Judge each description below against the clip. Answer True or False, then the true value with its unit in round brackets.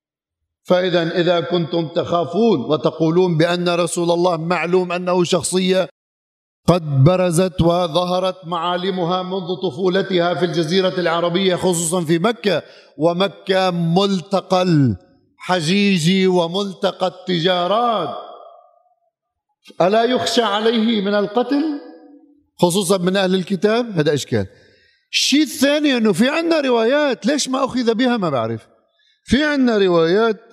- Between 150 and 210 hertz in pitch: True (185 Hz)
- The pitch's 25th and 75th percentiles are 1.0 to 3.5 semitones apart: False (4.7 semitones)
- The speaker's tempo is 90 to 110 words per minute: True (105 wpm)